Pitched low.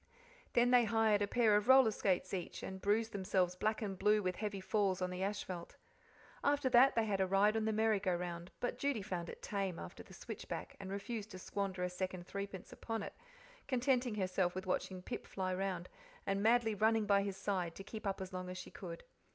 No: high, 200 Hz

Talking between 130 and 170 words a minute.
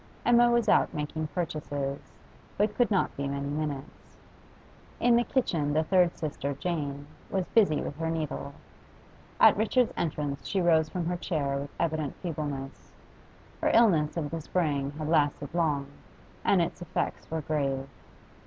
Yes: average, 155 wpm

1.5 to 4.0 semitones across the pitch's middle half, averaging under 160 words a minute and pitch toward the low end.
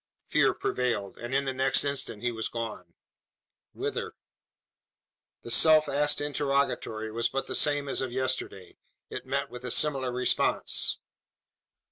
Yes: average, 3.0 semitones; average, 140 wpm; low, 130 Hz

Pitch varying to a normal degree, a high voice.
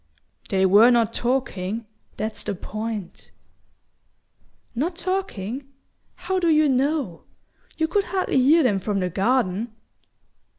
No: wide, 6.9 semitones; high, 240 Hz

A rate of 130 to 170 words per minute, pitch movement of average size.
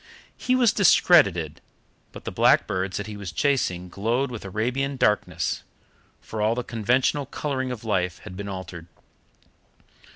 No: average, 140 wpm; wide, 6.0 semitones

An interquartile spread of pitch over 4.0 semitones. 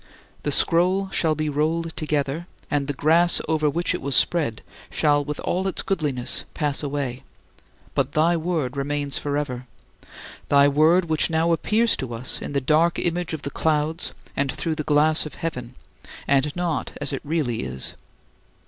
No: average, 2.9 semitones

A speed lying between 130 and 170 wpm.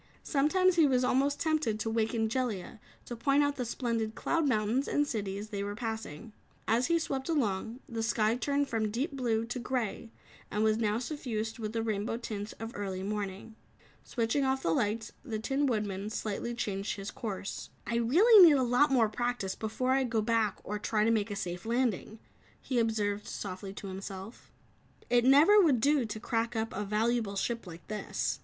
No: average, 190 wpm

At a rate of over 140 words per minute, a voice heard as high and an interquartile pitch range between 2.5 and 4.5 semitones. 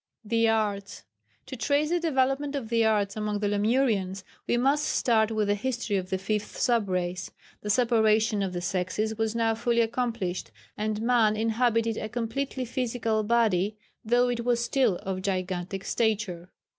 Yes: average, 170 wpm; high, 220 Hz; average, 2.9 semitones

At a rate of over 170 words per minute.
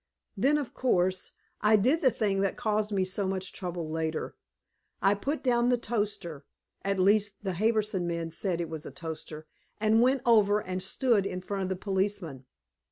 Yes: average, 180 wpm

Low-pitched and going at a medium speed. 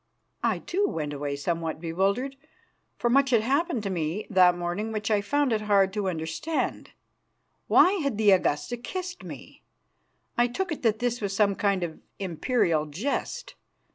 No: high, 205 Hz; average, 165 wpm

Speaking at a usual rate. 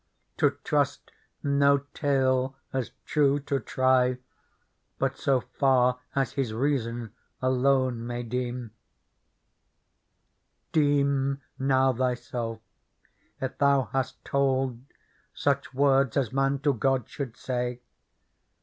No: slow, 105 wpm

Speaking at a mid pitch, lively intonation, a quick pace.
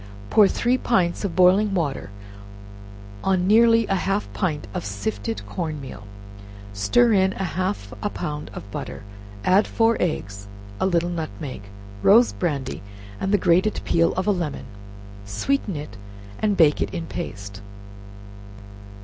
No: medium, 175 Hz; wide, 7.0 semitones; average, 140 wpm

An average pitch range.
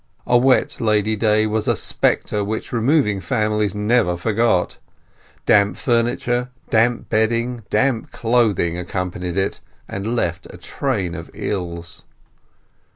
Yes: average, 3.5 semitones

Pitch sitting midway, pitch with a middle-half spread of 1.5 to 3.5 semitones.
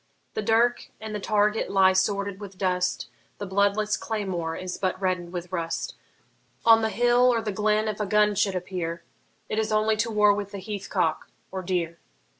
No: high, 200 Hz; narrow, 2.5 semitones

